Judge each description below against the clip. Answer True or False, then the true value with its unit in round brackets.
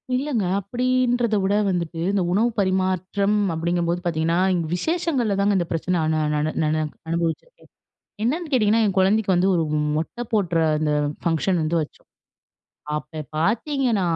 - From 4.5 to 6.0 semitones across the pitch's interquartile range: True (5.4 semitones)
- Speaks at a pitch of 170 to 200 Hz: True (190 Hz)